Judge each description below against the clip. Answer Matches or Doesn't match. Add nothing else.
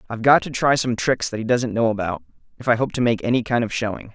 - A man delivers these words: Matches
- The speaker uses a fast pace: Matches